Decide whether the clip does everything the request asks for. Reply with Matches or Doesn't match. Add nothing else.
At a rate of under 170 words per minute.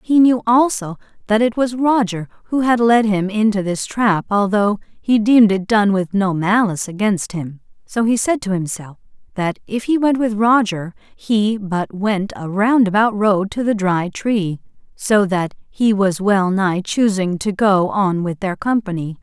Doesn't match